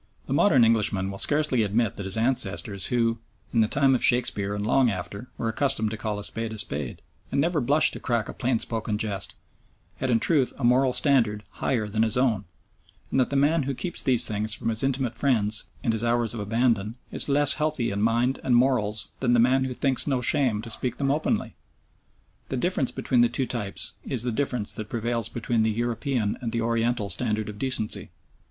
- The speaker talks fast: Yes, fast, 210 wpm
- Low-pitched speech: Yes, low, 120 Hz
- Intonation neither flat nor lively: Yes, average, 3.3 semitones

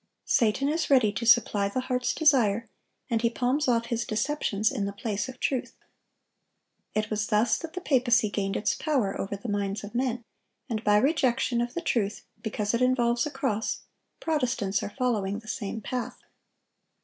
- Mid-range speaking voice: No, high, 235 Hz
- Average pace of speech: Yes, average, 175 wpm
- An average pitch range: Yes, average, 3.5 semitones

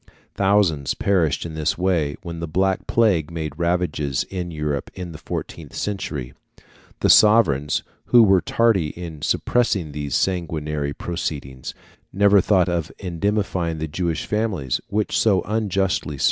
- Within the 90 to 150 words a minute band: Yes, average, 140 wpm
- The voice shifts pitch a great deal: No, average, 4.3 semitones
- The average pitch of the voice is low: Yes, very low, 85 Hz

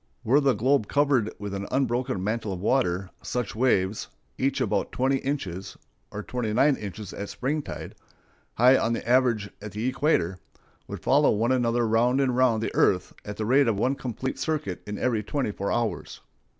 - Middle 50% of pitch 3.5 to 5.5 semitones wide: Yes, average, 4.1 semitones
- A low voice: Yes, low, 120 Hz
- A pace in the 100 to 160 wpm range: No, average, 180 wpm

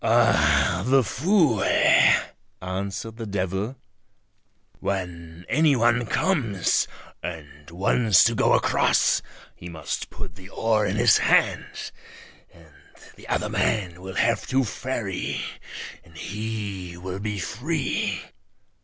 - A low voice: Yes, low, 100 Hz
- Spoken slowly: Yes, slow, 115 wpm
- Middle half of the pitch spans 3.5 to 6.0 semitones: Yes, average, 4.5 semitones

